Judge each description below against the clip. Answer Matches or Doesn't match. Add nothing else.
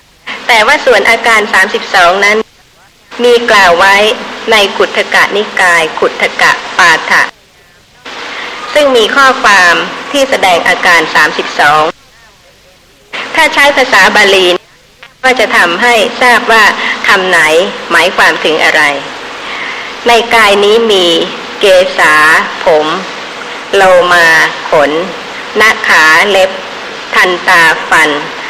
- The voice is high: Matches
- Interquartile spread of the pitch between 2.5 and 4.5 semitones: Doesn't match